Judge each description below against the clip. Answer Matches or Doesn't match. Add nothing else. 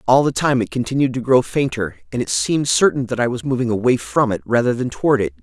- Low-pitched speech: Matches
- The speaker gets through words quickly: Matches